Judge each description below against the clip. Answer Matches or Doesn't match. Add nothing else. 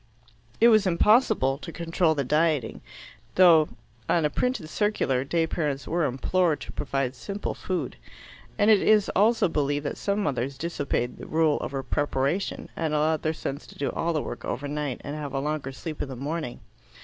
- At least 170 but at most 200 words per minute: Matches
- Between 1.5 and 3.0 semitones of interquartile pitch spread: Doesn't match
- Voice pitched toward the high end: Doesn't match